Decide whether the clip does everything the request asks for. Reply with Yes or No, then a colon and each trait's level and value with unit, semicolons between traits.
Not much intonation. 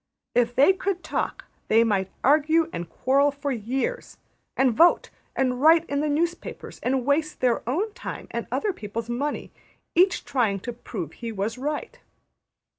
No: wide, 5.5 semitones